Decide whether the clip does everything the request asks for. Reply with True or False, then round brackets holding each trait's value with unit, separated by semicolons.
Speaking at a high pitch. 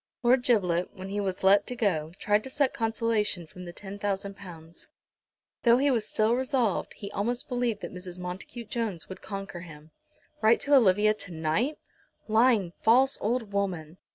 True (205 Hz)